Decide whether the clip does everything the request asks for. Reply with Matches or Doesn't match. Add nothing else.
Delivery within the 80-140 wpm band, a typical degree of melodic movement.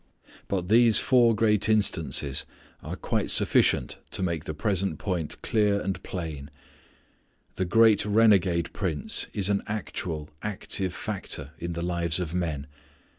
Matches